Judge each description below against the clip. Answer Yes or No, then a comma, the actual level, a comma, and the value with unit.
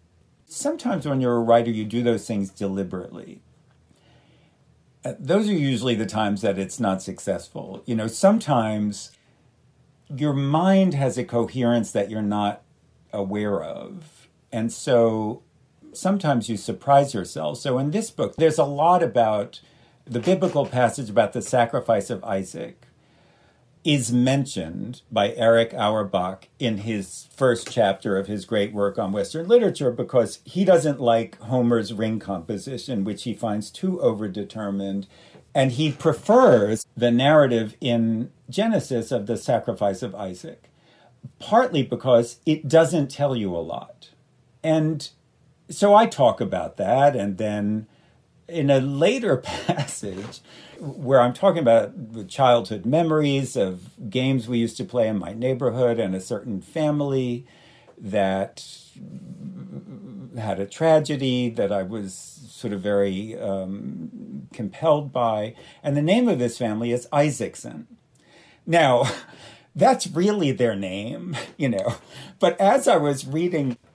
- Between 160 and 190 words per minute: No, slow, 135 wpm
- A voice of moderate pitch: No, low, 120 Hz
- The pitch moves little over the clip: No, wide, 5.4 semitones